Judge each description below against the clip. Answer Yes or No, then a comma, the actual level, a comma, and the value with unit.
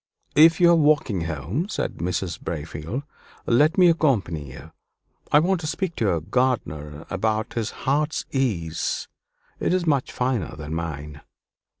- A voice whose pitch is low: Yes, low, 110 Hz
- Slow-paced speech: No, average, 145 wpm